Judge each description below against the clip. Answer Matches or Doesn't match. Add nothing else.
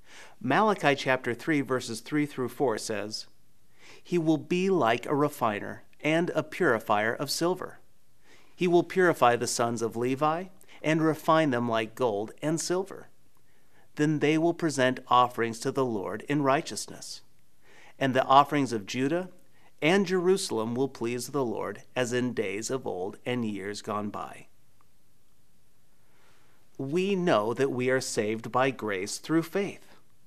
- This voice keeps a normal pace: Matches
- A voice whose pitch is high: Doesn't match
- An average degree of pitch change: Matches